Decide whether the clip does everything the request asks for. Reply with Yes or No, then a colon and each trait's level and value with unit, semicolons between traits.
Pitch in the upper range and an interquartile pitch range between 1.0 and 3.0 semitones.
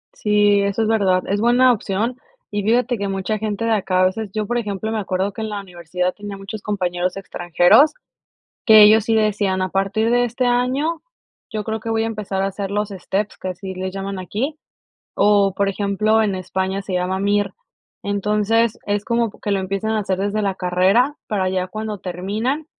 Yes: high, 205 Hz; narrow, 2.4 semitones